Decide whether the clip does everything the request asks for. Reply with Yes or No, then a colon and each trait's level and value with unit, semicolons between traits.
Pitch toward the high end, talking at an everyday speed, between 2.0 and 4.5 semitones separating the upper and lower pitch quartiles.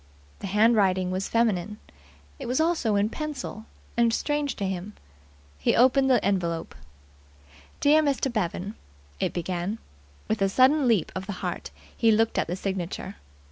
No: high, 215 Hz; average, 150 wpm; average, 5.2 semitones